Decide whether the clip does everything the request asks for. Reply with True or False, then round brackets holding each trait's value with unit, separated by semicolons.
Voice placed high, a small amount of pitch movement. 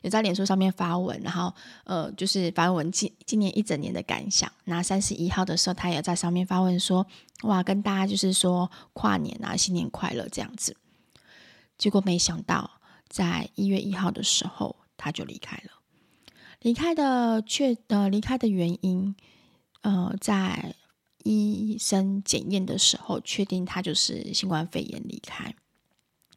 True (195 Hz; 2.3 semitones)